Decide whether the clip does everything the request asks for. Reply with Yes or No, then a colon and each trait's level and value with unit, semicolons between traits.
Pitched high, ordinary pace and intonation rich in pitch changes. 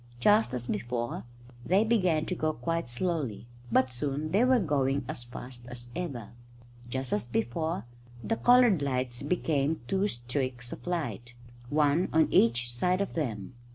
No: medium, 140 Hz; average, 155 wpm; wide, 6.1 semitones